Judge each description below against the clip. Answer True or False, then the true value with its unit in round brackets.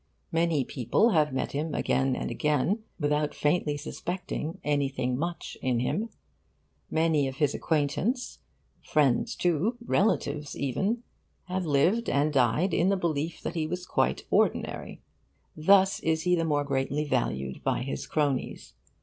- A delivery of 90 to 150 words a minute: True (140 wpm)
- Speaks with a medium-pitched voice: True (150 Hz)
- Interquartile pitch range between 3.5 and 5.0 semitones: True (4.0 semitones)